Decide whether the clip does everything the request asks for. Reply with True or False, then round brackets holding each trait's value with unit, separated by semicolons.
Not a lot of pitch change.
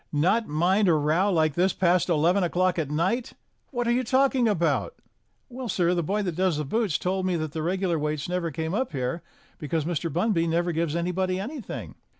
False (3.6 semitones)